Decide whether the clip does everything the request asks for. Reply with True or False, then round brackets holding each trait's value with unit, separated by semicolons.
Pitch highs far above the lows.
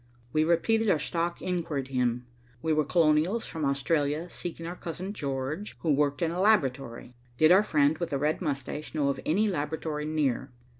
False (3.4 semitones)